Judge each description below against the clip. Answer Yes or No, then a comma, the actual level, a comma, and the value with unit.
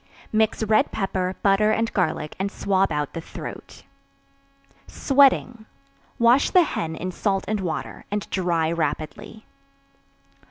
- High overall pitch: Yes, high, 195 Hz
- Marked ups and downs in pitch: No, average, 4.4 semitones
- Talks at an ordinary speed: No, slow, 125 wpm